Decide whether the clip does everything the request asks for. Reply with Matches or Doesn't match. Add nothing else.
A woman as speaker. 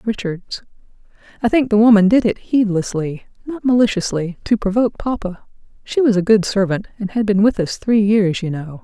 Matches